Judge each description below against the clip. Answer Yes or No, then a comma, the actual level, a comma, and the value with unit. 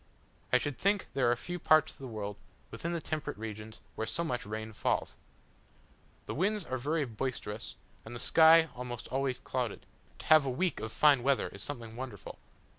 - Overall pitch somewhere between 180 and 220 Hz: No, low, 130 Hz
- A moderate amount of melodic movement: No, wide, 5.8 semitones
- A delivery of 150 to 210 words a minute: Yes, average, 190 wpm